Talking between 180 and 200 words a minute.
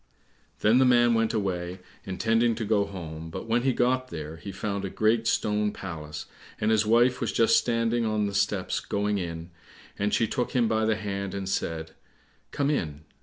Yes: average, 190 wpm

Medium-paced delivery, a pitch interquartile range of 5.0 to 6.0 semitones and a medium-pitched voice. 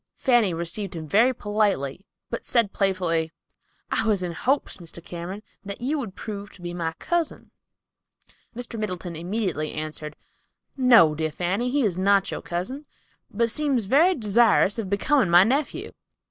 No: average, 160 wpm; wide, 5.4 semitones; high, 200 Hz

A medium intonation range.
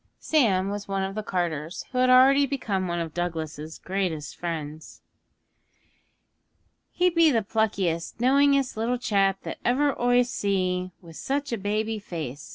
No: wide, 6.2 semitones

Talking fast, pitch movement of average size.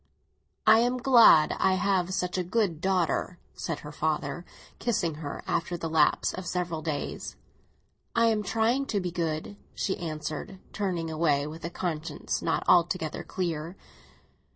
No: average, 150 wpm; average, 3.6 semitones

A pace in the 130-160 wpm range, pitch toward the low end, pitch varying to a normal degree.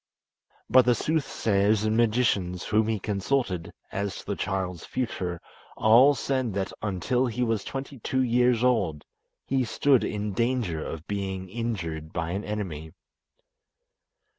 Yes: average, 140 wpm; low, 105 Hz; average, 4.8 semitones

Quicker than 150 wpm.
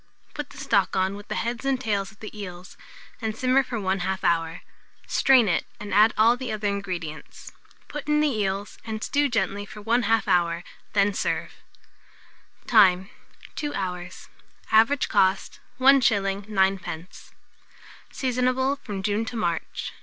No: average, 145 wpm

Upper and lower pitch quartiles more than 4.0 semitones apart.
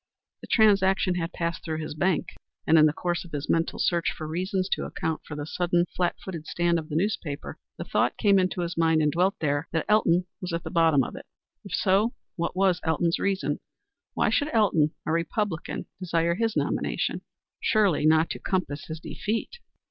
No: average, 3.0 semitones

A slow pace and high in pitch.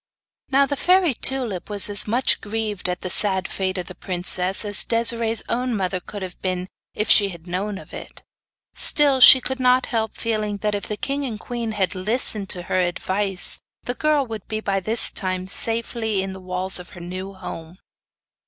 No: average, 195 wpm; high, 205 Hz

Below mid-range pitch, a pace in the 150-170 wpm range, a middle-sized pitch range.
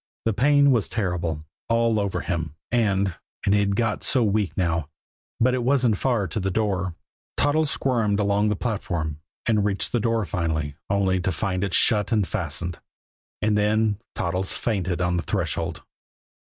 Yes: low, 100 Hz; average, 165 wpm; average, 3.9 semitones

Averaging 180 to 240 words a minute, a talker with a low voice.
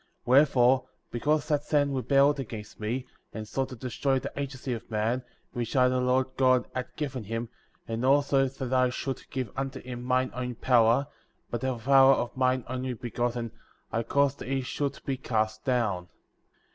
Yes: average, 185 wpm; low, 130 Hz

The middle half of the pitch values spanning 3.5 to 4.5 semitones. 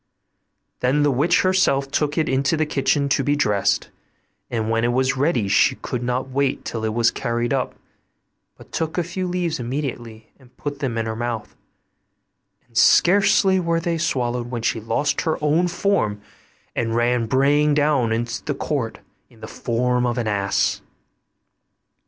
Yes: average, 4.2 semitones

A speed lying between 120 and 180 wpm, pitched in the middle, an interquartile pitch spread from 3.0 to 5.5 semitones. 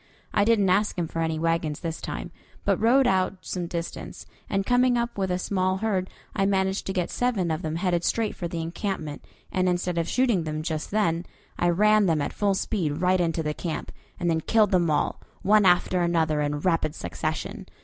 No: fast, 205 wpm; medium, 180 Hz; average, 3.4 semitones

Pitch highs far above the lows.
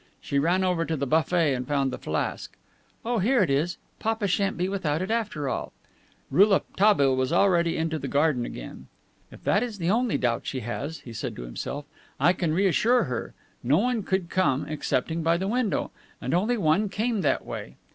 Yes: wide, 6.0 semitones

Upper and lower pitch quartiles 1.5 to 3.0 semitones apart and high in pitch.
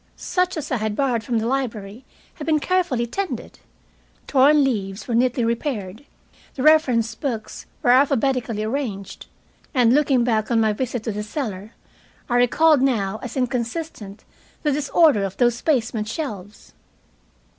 No: average, 4.3 semitones; high, 245 Hz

